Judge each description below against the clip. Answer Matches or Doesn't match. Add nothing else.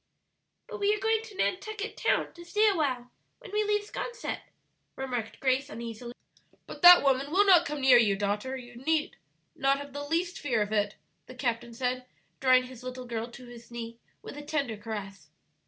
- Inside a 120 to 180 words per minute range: Doesn't match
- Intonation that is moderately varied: Doesn't match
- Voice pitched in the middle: Doesn't match